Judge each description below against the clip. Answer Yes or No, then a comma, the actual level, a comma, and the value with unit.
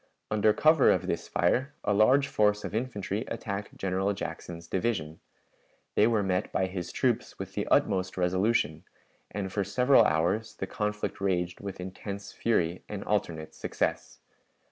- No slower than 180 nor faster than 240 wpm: No, average, 150 wpm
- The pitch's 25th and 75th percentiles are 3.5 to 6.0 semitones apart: No, average, 2.8 semitones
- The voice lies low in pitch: Yes, low, 100 Hz